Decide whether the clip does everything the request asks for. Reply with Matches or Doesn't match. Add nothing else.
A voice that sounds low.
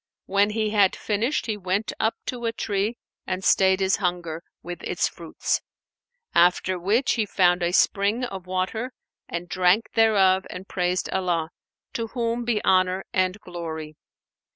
Doesn't match